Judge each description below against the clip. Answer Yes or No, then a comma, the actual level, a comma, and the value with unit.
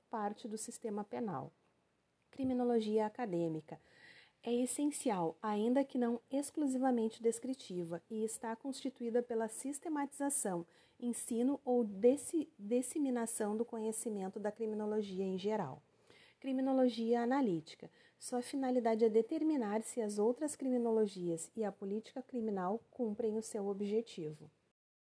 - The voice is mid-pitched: No, high, 230 Hz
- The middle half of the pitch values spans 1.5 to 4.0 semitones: Yes, average, 3.6 semitones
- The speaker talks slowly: Yes, slow, 110 wpm